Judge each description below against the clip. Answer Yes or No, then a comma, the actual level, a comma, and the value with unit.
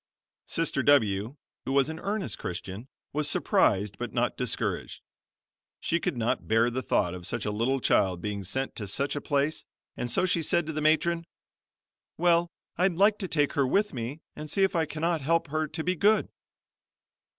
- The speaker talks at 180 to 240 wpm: Yes, average, 185 wpm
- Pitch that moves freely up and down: Yes, wide, 6.3 semitones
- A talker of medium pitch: Yes, medium, 145 Hz